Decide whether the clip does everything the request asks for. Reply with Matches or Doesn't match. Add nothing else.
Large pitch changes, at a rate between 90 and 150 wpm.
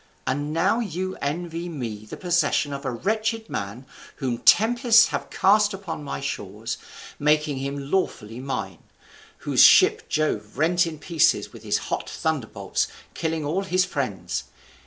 Matches